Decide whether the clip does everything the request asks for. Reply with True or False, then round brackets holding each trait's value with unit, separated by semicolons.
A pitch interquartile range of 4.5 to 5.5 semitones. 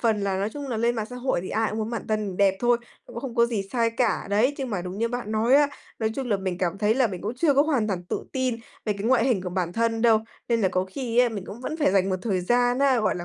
False (3.8 semitones)